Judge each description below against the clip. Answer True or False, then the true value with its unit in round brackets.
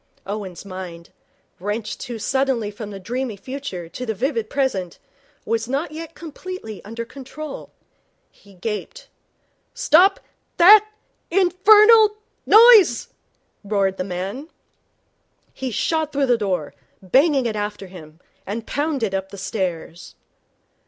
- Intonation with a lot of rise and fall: True (7.7 semitones)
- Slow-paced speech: True (120 wpm)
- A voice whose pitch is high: True (230 Hz)